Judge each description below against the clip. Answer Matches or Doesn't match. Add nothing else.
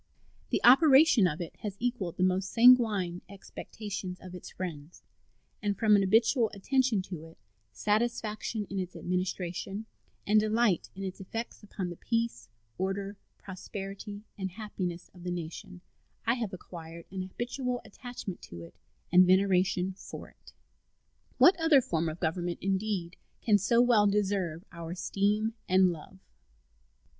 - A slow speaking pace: Doesn't match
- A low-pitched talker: Doesn't match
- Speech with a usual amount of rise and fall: Matches